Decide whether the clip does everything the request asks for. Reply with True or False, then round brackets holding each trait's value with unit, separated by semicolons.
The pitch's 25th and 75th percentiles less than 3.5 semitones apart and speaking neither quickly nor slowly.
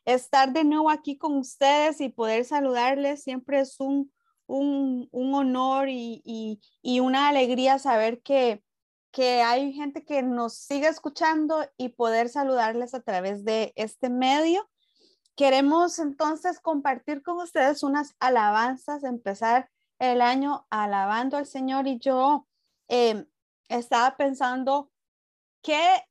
False (2.9 semitones; 130 wpm)